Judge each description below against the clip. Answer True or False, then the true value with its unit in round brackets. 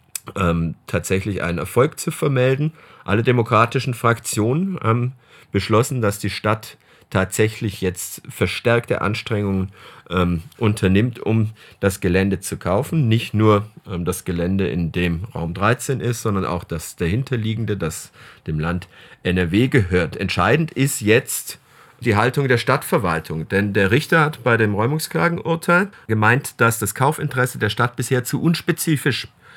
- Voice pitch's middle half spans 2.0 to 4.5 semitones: False (5.1 semitones)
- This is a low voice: True (110 Hz)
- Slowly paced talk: False (140 wpm)